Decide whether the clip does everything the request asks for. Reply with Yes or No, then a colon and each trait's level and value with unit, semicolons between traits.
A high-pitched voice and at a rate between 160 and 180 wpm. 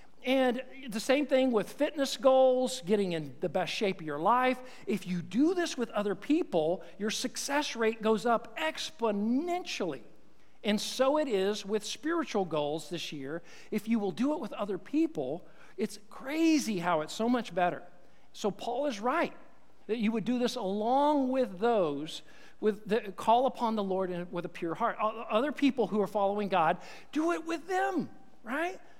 Yes: high, 225 Hz; average, 175 wpm